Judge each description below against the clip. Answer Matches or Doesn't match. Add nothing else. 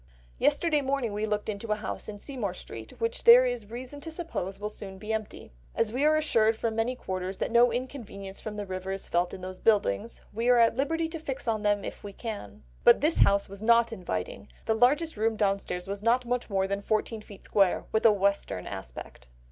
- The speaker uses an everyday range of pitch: Matches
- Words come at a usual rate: Doesn't match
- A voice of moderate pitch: Doesn't match